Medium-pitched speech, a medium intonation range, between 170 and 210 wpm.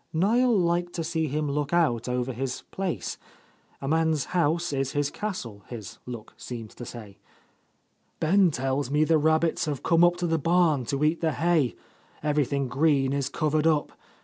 Yes: medium, 150 Hz; average, 3.8 semitones; average, 175 wpm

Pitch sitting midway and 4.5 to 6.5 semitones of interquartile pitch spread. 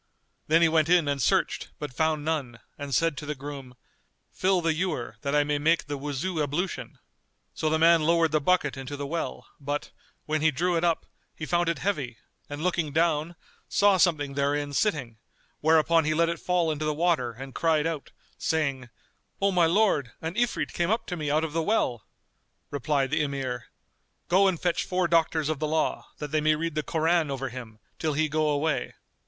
No: medium, 155 Hz; average, 2.8 semitones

